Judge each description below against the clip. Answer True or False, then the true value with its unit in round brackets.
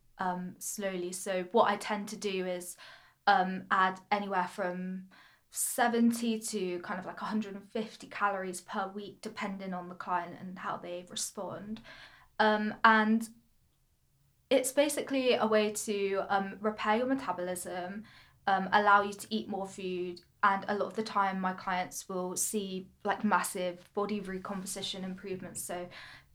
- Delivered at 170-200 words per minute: False (145 wpm)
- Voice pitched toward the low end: False (195 Hz)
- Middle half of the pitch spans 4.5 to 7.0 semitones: False (2.5 semitones)